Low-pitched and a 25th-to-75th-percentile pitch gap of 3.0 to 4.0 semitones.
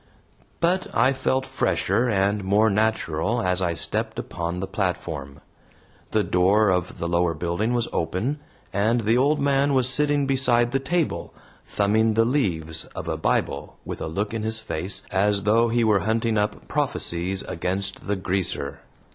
No: low, 105 Hz; average, 4.6 semitones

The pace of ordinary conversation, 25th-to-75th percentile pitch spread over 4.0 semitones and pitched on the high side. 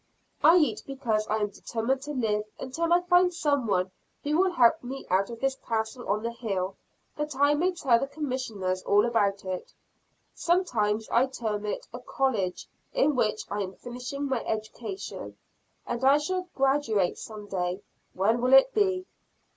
Yes: average, 170 wpm; wide, 5.6 semitones; high, 245 Hz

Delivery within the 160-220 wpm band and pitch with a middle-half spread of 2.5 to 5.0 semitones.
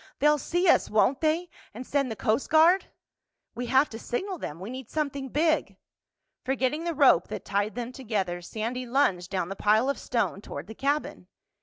No: average, 180 wpm; wide, 5.6 semitones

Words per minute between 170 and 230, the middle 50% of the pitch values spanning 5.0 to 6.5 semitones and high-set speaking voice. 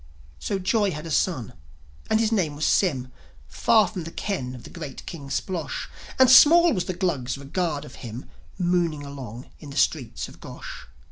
No: average, 185 wpm; wide, 5.5 semitones; medium, 165 Hz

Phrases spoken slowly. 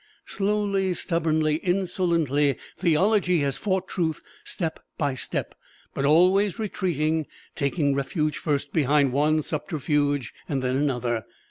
Yes: slow, 110 wpm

